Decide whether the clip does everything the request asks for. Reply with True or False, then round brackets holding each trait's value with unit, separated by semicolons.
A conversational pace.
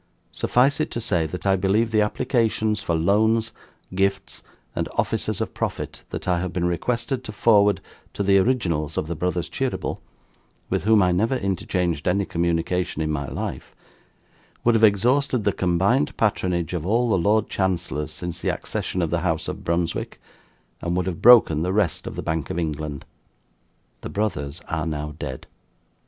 True (175 wpm)